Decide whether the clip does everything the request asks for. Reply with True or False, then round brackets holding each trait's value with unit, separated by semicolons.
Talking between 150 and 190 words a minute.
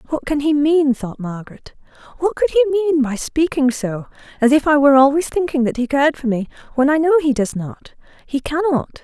False (205 wpm)